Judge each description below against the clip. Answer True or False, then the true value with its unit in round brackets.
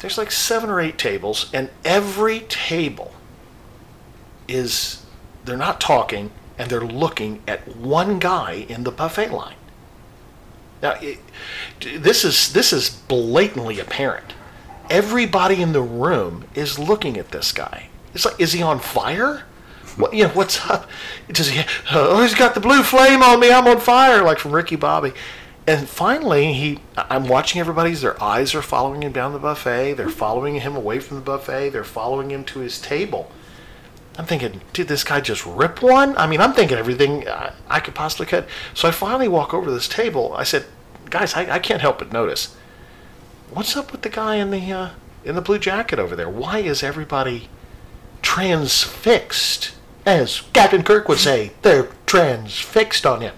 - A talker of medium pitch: True (165 Hz)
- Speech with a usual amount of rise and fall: False (8.0 semitones)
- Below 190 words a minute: True (175 wpm)